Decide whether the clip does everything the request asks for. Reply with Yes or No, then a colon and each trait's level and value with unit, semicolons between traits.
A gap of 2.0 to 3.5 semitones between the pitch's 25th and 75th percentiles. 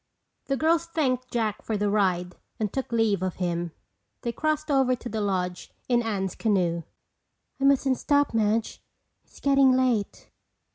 No: average, 5.3 semitones